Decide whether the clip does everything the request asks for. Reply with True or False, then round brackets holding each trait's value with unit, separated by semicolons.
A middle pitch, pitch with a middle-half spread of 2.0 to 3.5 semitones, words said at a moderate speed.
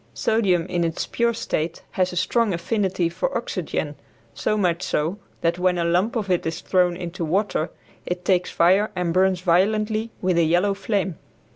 True (180 Hz; 2.9 semitones; 175 wpm)